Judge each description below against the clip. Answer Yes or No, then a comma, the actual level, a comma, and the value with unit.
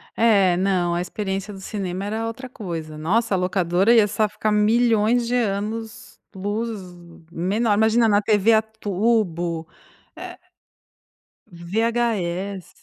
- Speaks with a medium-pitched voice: No, high, 205 Hz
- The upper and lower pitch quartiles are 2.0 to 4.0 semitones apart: Yes, average, 3.4 semitones